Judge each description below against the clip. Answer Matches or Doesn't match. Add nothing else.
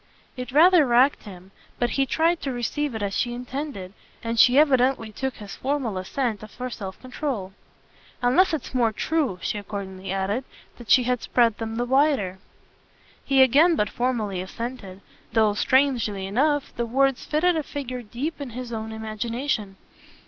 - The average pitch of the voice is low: Doesn't match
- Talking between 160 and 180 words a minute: Matches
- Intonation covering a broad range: Doesn't match